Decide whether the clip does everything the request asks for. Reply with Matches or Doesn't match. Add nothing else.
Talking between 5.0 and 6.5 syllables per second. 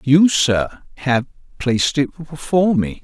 Doesn't match